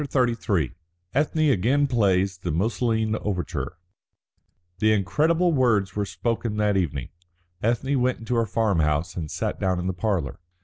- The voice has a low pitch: Yes, low, 105 Hz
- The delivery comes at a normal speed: Yes, average, 150 wpm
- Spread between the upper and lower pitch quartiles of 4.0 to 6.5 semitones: Yes, average, 5.0 semitones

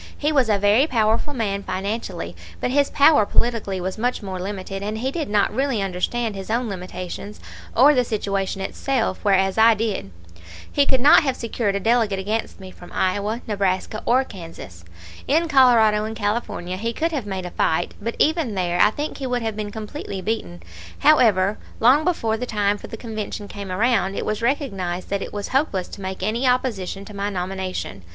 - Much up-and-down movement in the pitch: No, average, 4.1 semitones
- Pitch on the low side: No, high, 215 Hz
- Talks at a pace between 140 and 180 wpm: No, average, 190 wpm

